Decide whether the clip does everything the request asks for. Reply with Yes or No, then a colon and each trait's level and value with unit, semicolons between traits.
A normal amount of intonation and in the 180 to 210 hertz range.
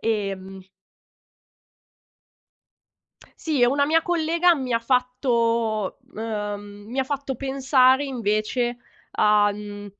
No: average, 4.5 semitones; high, 240 Hz